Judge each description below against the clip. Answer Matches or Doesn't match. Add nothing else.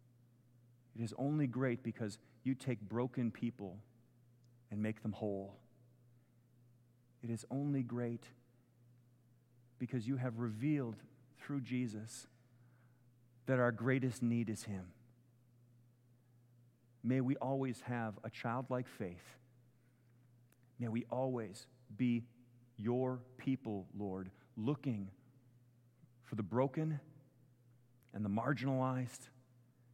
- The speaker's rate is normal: Doesn't match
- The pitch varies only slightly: Matches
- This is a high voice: Doesn't match